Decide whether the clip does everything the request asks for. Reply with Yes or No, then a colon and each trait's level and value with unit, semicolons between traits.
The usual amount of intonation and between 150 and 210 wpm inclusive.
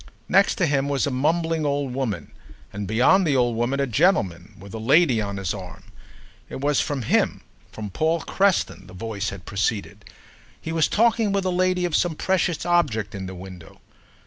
No: wide, 8.5 semitones; average, 185 wpm